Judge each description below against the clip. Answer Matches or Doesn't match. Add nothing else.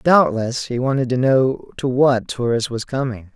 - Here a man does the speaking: Matches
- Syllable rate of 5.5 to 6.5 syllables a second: Doesn't match